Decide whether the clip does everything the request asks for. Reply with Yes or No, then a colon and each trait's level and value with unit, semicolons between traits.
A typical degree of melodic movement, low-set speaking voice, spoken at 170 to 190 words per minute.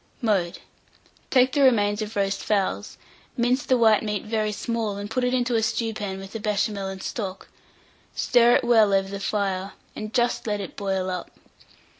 No: average, 3.0 semitones; high, 210 Hz; average, 180 wpm